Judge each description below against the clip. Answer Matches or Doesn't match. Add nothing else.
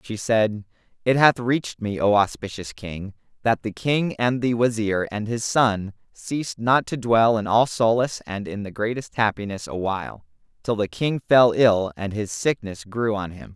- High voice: Doesn't match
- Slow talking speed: Doesn't match